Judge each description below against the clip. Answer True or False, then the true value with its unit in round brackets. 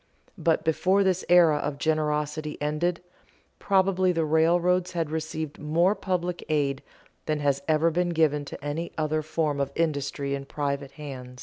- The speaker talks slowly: False (150 wpm)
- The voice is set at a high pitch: False (155 Hz)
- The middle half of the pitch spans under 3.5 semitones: True (2.8 semitones)